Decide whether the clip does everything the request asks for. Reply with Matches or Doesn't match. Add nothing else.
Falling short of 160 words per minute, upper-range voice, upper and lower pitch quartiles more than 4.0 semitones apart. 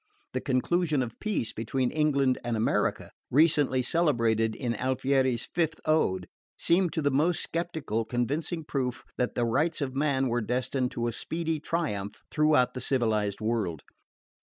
Doesn't match